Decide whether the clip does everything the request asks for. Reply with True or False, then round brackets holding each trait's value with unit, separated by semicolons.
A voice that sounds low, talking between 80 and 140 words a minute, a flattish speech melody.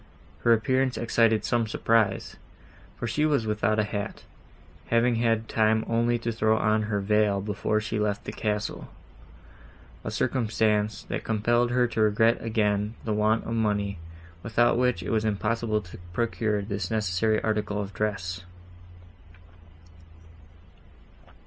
True (110 Hz; 135 wpm; 1.7 semitones)